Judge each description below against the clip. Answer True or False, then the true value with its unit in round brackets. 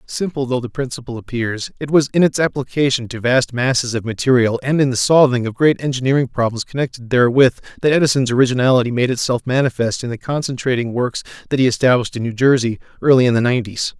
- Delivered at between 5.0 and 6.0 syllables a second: False (6.5 syllables/s)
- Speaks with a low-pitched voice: True (125 Hz)